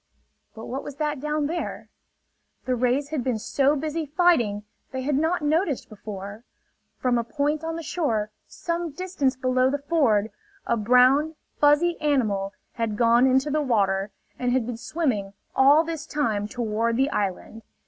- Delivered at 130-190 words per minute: Yes, average, 160 wpm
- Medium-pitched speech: No, very high, 265 Hz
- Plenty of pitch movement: No, average, 4.8 semitones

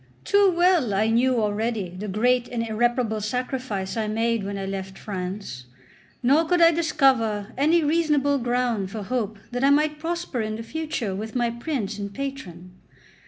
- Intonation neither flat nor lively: Yes, average, 5.0 semitones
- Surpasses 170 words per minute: No, average, 165 wpm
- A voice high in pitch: Yes, high, 235 Hz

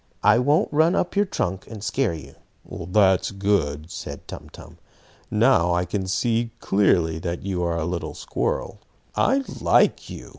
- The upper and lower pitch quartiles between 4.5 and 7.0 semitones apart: Yes, average, 5.3 semitones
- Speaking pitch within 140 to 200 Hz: No, very low, 95 Hz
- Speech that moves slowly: No, average, 160 wpm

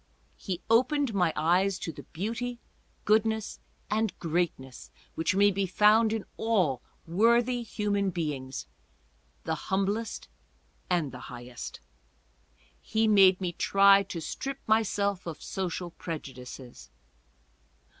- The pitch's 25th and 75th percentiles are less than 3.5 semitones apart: No, average, 4.9 semitones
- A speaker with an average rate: No, slow, 115 wpm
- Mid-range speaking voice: No, high, 195 Hz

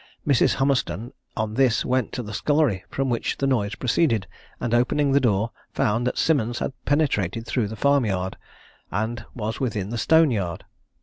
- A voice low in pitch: Yes, low, 120 Hz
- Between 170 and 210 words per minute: Yes, average, 175 wpm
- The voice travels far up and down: No, average, 4.2 semitones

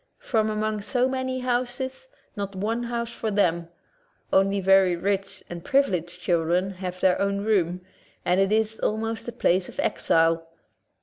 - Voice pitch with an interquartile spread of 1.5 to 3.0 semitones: No, average, 4.1 semitones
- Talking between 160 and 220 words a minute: No, average, 150 wpm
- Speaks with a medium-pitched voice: No, high, 200 Hz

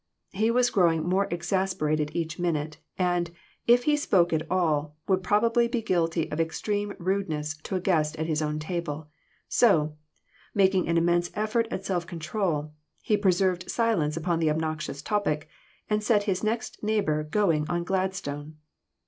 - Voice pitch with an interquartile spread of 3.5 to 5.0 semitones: Yes, average, 4.4 semitones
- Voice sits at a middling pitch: Yes, medium, 175 Hz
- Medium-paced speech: Yes, average, 160 wpm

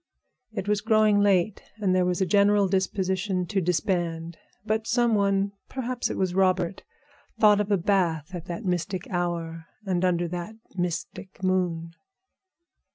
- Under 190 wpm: Yes, average, 150 wpm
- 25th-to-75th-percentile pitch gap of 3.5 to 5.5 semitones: No, narrow, 2.6 semitones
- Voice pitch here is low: No, medium, 185 Hz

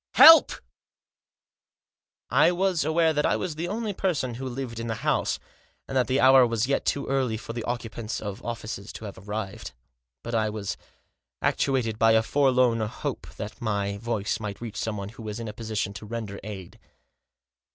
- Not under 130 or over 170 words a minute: No, average, 185 wpm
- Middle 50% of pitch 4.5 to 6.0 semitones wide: No, average, 3.8 semitones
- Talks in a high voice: No, low, 115 Hz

